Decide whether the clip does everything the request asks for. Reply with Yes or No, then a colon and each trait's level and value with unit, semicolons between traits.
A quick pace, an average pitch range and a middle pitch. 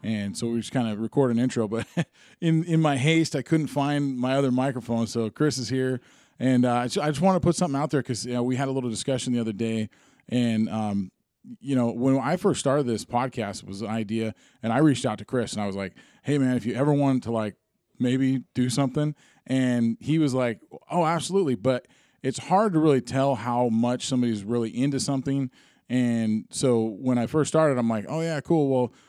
No: fast, 230 wpm; average, 3.7 semitones; low, 130 Hz